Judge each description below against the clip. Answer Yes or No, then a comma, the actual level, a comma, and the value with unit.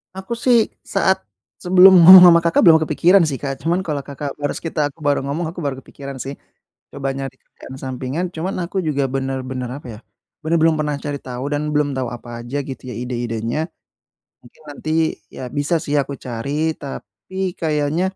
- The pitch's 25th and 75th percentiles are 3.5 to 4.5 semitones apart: Yes, average, 4.1 semitones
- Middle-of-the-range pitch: Yes, medium, 145 Hz